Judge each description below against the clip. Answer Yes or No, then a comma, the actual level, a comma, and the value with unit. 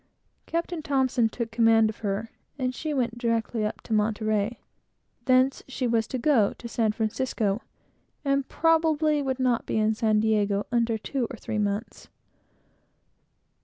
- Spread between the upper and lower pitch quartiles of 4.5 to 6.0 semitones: No, average, 3.3 semitones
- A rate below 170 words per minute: Yes, average, 155 wpm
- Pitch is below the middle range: No, high, 230 Hz